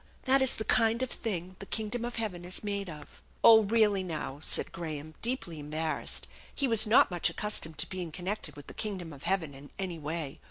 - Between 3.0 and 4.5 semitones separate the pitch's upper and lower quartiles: No, wide, 5.5 semitones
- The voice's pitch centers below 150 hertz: No, medium, 185 Hz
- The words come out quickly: Yes, fast, 215 wpm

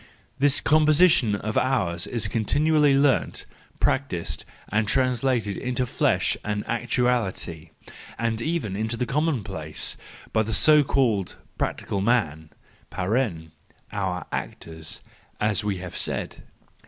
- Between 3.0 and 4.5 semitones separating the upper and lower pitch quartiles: No, average, 5.1 semitones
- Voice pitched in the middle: No, low, 115 Hz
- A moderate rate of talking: No, slow, 110 wpm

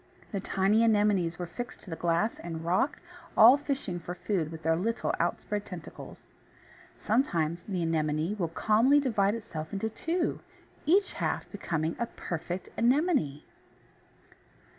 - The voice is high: Yes, high, 195 Hz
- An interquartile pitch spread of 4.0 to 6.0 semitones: Yes, wide, 5.6 semitones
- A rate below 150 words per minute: Yes, average, 140 wpm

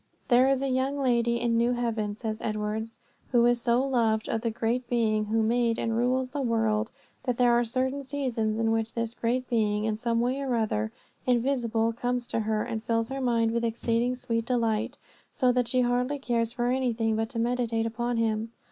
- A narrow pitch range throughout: Yes, narrow, 1.8 semitones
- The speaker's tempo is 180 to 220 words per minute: Yes, average, 200 wpm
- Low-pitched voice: No, high, 235 Hz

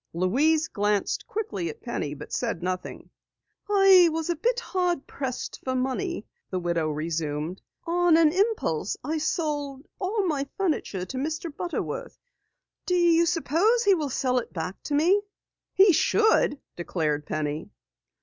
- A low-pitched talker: No, very high, 295 Hz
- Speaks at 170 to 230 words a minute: No, average, 145 wpm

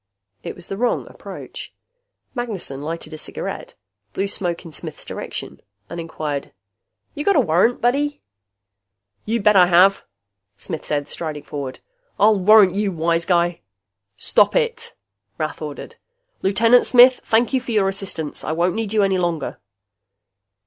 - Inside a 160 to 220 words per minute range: No, average, 150 wpm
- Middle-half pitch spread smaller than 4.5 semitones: No, average, 5.1 semitones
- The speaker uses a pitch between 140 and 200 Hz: Yes, medium, 185 Hz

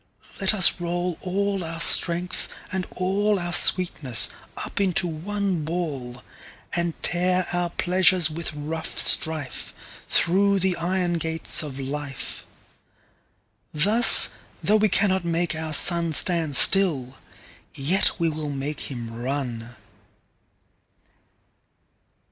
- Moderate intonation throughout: Yes, average, 3.8 semitones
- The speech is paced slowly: Yes, slow, 100 wpm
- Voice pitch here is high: No, medium, 170 Hz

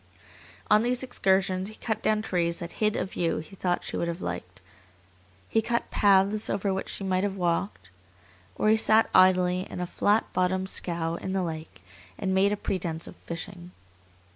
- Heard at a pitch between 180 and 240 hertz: Yes, high, 190 Hz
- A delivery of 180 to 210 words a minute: Yes, average, 185 wpm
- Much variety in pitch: No, average, 2.9 semitones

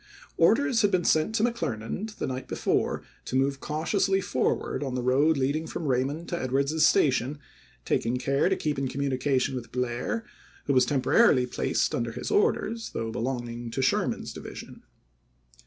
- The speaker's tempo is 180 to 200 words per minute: No, average, 165 wpm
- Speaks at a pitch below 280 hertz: Yes, medium, 140 Hz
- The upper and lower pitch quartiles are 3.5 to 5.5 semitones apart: Yes, average, 4.6 semitones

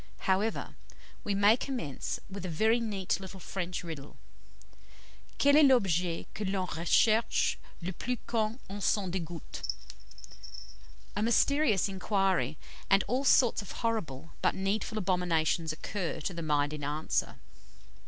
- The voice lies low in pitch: No, high, 190 Hz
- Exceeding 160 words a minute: No, slow, 135 wpm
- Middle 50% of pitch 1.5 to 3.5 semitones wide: No, average, 4.6 semitones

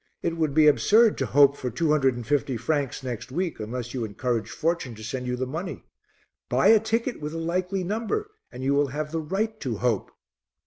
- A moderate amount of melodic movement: No, wide, 5.7 semitones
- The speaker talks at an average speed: No, fast, 215 wpm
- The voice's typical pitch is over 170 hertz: No, medium, 145 Hz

